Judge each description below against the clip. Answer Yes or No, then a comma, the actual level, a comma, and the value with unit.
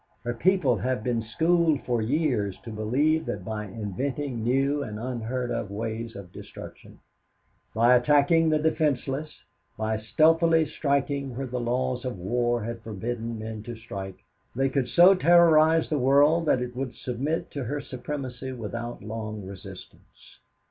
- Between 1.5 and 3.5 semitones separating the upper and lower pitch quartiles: No, average, 4.5 semitones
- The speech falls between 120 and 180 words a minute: Yes, average, 150 wpm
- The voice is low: Yes, low, 125 Hz